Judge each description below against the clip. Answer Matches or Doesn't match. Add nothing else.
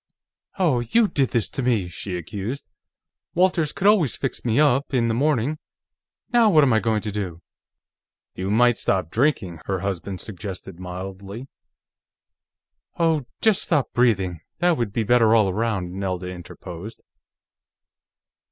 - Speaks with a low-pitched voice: Matches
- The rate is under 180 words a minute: Matches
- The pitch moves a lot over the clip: Matches